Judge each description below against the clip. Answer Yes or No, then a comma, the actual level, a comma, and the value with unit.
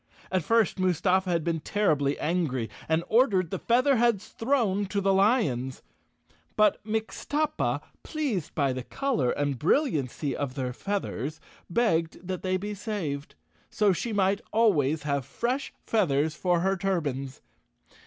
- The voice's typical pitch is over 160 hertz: Yes, medium, 185 Hz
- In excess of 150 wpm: No, average, 140 wpm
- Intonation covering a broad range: Yes, wide, 6.6 semitones